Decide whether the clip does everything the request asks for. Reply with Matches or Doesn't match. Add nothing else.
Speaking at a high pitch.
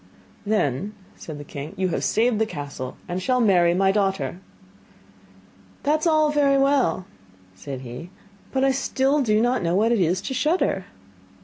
Matches